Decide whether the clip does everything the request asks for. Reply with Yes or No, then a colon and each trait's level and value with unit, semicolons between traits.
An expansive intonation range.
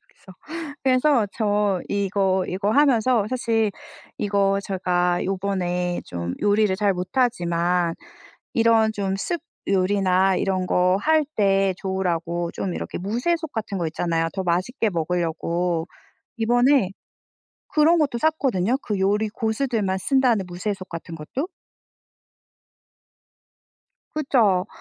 No: average, 4.2 semitones